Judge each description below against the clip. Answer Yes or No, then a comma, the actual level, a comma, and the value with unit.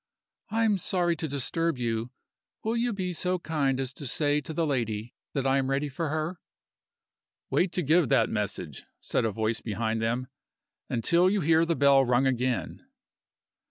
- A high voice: No, medium, 140 Hz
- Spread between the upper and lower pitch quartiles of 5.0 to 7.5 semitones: Yes, wide, 5.5 semitones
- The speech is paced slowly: No, average, 175 wpm